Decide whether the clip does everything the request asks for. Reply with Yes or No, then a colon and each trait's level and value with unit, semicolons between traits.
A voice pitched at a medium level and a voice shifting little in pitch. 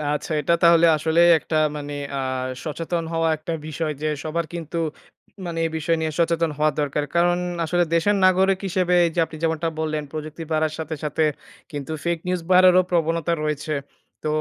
Yes: medium, 165 Hz; narrow, 1.7 semitones